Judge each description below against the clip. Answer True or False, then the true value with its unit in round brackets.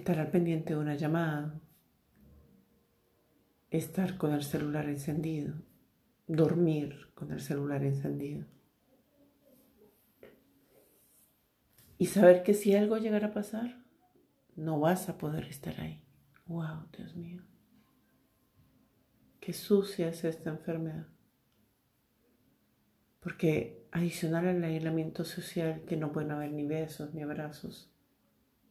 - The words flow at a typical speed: False (105 wpm)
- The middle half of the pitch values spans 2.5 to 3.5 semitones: True (2.9 semitones)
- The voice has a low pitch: False (165 Hz)